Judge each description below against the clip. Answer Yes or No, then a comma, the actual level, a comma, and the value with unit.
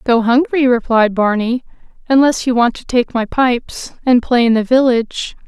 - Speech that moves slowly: No, average, 175 wpm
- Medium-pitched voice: No, high, 245 Hz